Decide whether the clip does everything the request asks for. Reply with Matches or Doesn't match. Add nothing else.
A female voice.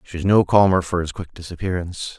Doesn't match